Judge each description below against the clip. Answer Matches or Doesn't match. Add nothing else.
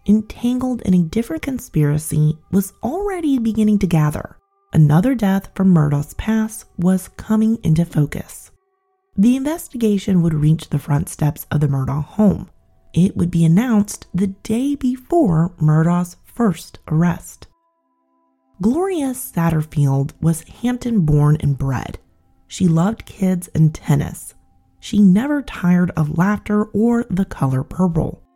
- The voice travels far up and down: Matches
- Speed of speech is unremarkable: Doesn't match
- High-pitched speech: Doesn't match